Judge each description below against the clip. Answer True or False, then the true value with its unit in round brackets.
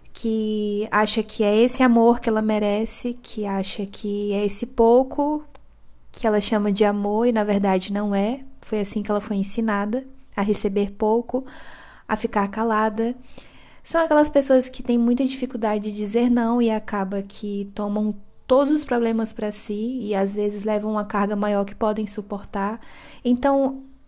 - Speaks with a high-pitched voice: True (215 Hz)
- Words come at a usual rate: True (165 wpm)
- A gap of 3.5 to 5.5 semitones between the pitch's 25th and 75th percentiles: False (2.8 semitones)